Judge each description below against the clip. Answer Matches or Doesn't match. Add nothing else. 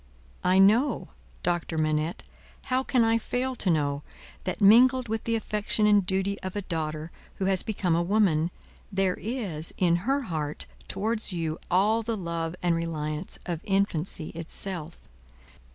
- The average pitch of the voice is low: Doesn't match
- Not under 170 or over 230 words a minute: Doesn't match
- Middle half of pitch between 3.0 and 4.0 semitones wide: Doesn't match